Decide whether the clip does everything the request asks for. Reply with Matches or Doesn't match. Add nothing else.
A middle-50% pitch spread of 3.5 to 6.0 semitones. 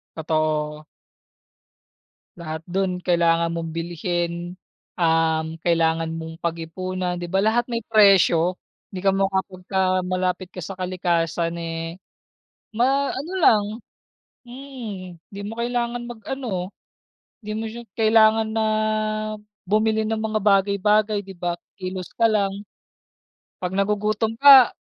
Matches